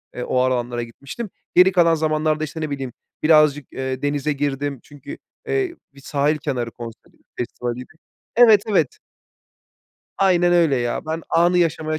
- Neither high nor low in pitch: Yes, medium, 150 Hz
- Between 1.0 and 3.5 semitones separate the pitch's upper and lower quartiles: No, average, 4.0 semitones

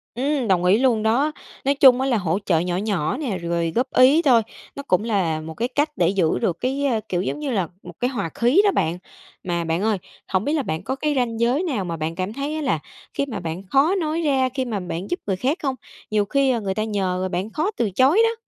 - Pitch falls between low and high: No, high, 230 Hz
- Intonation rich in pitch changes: Yes, wide, 7.0 semitones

